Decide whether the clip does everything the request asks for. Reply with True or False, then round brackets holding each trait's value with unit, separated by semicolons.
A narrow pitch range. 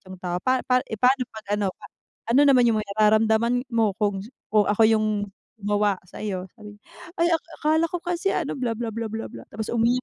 False (3.2 semitones)